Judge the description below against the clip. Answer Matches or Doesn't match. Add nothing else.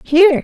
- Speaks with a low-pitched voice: Doesn't match